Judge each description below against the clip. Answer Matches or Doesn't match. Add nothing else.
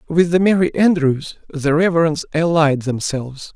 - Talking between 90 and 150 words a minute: Matches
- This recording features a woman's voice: Doesn't match